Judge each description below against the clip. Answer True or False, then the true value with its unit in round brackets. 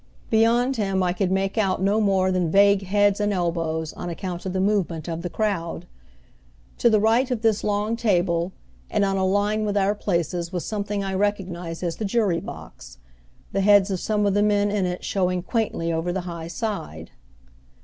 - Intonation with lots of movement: False (2.9 semitones)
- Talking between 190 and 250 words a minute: True (195 wpm)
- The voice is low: False (195 Hz)